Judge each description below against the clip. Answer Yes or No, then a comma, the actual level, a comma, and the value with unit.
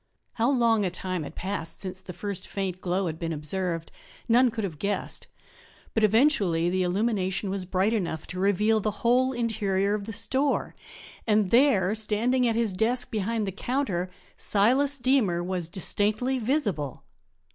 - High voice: Yes, high, 205 Hz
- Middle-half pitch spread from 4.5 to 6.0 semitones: No, average, 4.0 semitones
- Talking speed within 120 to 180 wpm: Yes, average, 160 wpm